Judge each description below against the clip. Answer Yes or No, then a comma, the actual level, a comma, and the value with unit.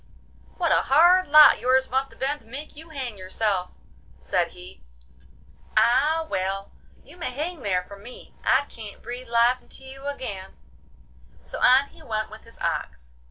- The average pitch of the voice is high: Yes, very high, 250 Hz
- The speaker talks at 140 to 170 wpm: Yes, average, 165 wpm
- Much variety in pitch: Yes, wide, 5.8 semitones